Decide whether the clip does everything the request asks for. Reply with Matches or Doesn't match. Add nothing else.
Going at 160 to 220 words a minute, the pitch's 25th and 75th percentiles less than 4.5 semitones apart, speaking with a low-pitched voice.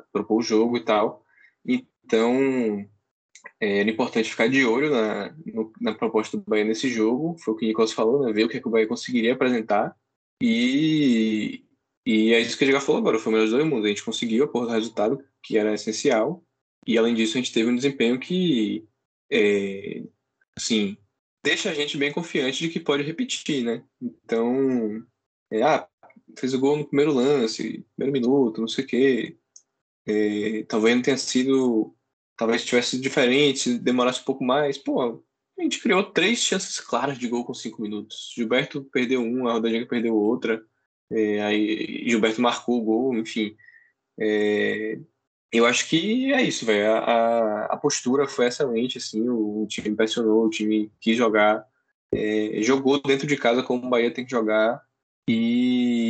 Matches